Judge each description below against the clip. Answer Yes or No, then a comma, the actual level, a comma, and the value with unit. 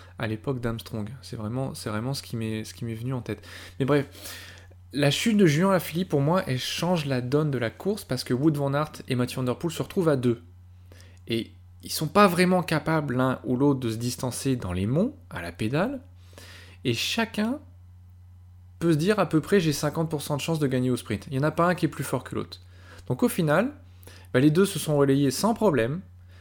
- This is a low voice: Yes, low, 130 Hz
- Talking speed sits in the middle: No, fast, 230 wpm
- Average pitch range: No, wide, 8.5 semitones